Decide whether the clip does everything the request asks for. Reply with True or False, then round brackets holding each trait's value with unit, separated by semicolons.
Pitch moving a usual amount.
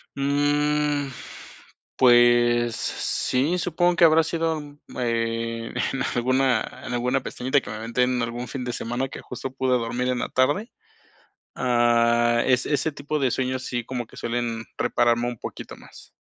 True (3.0 semitones)